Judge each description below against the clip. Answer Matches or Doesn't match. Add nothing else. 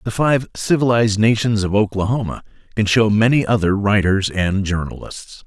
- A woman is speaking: Doesn't match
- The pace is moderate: Matches